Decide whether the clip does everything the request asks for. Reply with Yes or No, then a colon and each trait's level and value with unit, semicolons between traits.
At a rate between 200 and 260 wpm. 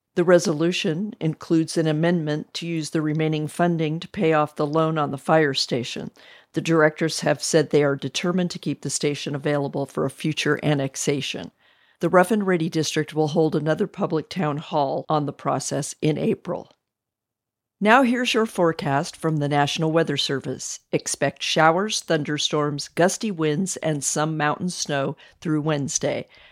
No: average, 160 wpm